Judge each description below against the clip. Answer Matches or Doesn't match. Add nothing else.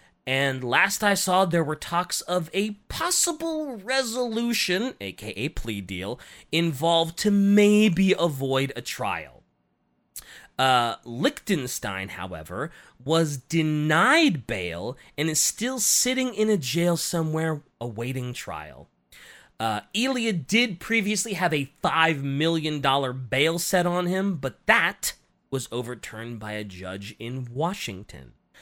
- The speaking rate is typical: Doesn't match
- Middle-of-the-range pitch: Matches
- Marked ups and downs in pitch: Matches